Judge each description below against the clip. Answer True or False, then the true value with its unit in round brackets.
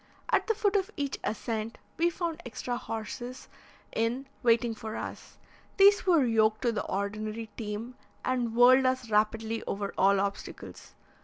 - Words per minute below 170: True (150 wpm)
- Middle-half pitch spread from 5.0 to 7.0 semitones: False (3.1 semitones)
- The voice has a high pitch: True (230 Hz)